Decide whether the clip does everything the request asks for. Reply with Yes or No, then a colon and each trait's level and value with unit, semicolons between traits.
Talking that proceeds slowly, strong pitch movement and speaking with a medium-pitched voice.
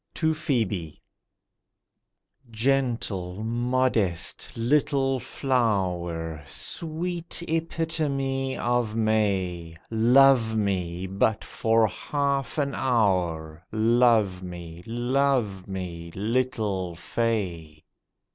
No: slow, 75 wpm; wide, 6.4 semitones; low, 110 Hz